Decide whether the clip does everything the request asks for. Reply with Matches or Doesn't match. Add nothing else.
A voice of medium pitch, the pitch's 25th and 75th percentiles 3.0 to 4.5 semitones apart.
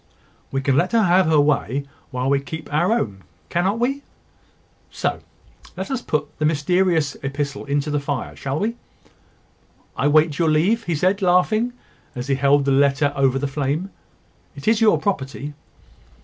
Doesn't match